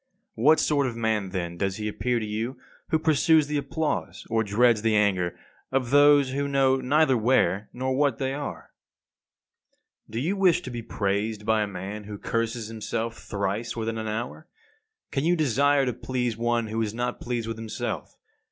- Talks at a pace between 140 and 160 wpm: No, average, 185 wpm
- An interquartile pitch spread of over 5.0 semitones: No, average, 4.2 semitones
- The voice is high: No, low, 115 Hz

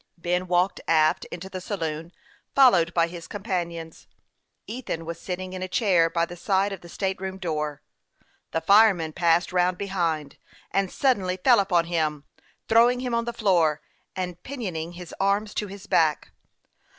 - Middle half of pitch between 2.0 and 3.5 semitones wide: Yes, average, 3.0 semitones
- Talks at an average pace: Yes, average, 165 wpm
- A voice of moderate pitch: Yes, medium, 180 Hz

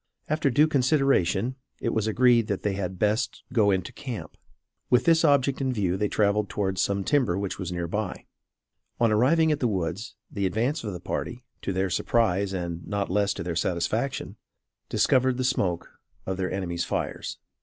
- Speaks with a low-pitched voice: Yes, low, 105 Hz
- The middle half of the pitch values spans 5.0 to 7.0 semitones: Yes, average, 5.3 semitones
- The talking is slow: No, average, 180 wpm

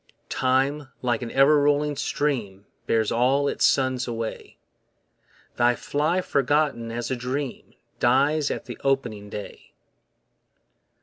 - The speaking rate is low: Yes, slow, 120 wpm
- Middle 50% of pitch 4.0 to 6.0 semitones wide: No, average, 3.3 semitones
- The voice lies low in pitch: Yes, low, 130 Hz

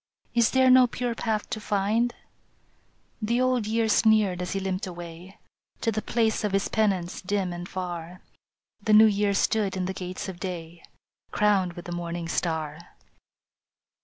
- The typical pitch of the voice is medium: No, high, 195 Hz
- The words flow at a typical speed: Yes, average, 165 wpm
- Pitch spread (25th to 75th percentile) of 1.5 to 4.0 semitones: Yes, average, 3.7 semitones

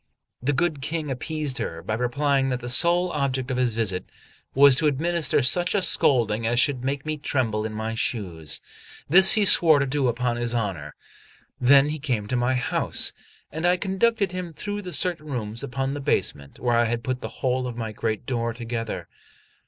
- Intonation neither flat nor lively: Yes, average, 4.5 semitones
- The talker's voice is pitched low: Yes, low, 130 Hz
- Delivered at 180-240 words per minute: Yes, average, 190 wpm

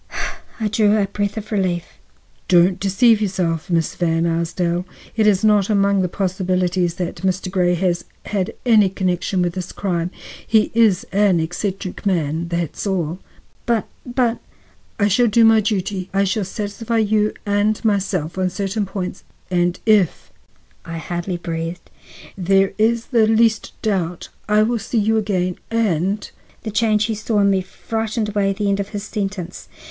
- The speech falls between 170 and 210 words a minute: No, average, 160 wpm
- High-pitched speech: Yes, high, 195 Hz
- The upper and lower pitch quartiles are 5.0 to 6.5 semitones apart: No, average, 3.1 semitones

